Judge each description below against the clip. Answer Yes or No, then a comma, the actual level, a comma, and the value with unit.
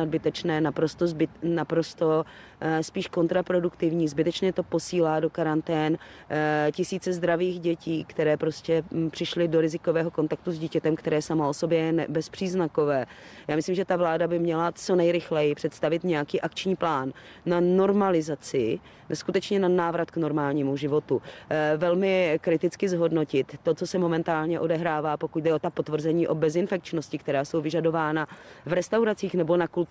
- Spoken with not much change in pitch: Yes, narrow, 1.9 semitones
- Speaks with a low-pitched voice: No, medium, 165 Hz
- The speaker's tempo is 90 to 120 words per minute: No, average, 145 wpm